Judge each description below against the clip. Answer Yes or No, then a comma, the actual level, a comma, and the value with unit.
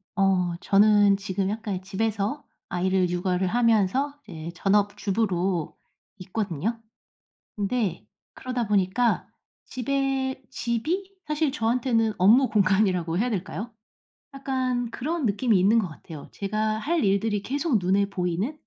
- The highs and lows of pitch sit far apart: No, average, 4.5 semitones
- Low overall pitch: No, high, 210 Hz